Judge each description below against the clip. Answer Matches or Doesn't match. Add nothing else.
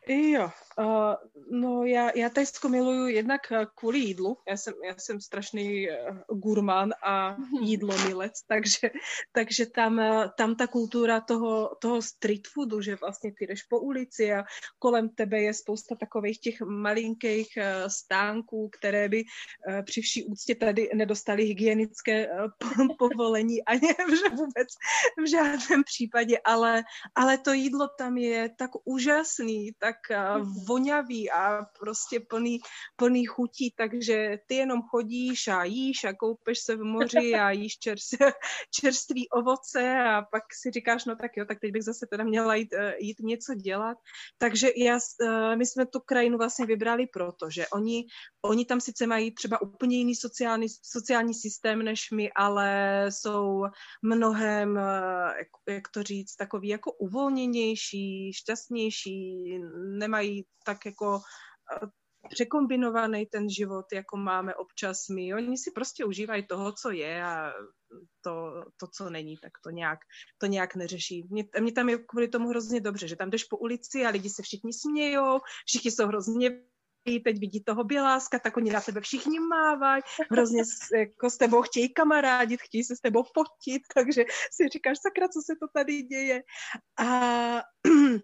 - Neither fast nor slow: Matches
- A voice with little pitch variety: Doesn't match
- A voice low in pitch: Doesn't match